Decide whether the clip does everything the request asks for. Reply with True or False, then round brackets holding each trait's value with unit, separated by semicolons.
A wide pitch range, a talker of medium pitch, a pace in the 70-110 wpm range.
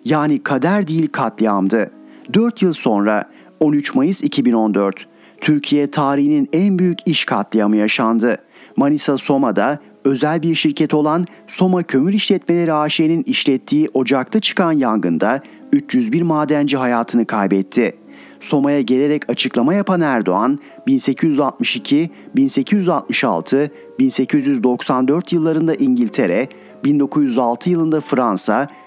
True (7.0 semitones; 155 Hz; 100 wpm)